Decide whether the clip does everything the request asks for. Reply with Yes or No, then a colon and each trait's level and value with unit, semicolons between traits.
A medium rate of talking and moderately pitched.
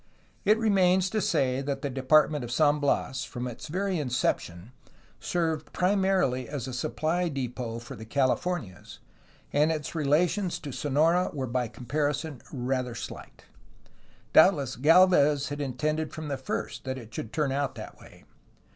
Yes: average, 155 wpm; medium, 145 Hz